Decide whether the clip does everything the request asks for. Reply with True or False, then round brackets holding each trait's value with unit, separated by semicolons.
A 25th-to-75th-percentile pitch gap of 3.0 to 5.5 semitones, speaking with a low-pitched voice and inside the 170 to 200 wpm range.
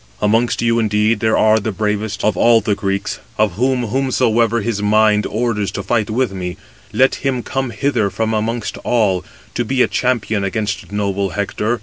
False (2.4 semitones; 110 Hz; 180 wpm)